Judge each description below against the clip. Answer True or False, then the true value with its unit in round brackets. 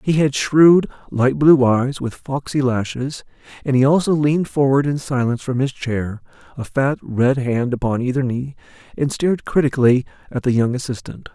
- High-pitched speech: False (130 Hz)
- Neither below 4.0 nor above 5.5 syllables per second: True (5.0 syllables/s)